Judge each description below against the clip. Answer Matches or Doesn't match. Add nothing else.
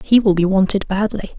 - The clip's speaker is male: Doesn't match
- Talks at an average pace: Doesn't match